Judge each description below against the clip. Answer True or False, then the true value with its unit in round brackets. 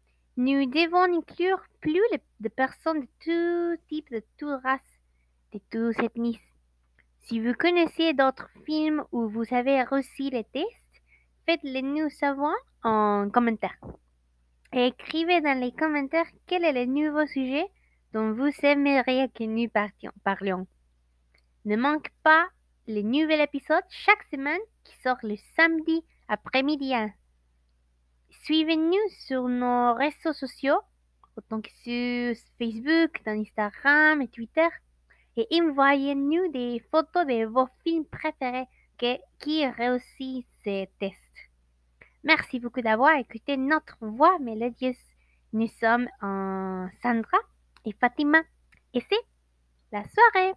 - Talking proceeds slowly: True (125 wpm)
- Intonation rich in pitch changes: True (5.8 semitones)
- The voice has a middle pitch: False (260 Hz)